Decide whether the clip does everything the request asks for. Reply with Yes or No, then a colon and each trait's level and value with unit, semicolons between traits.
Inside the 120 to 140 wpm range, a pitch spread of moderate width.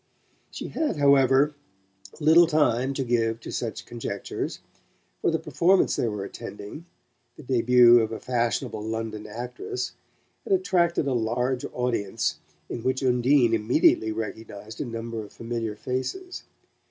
Yes: slow, 135 wpm; average, 3.7 semitones